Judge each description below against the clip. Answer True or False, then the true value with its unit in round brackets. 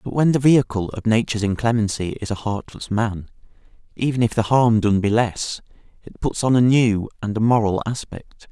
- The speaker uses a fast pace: False (190 wpm)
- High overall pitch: False (110 Hz)